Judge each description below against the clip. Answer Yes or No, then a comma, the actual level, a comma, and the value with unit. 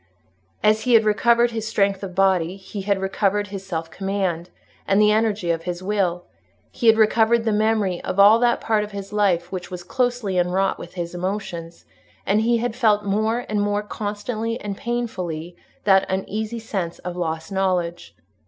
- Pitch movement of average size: Yes, average, 3.2 semitones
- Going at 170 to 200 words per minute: Yes, average, 180 wpm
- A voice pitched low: No, high, 200 Hz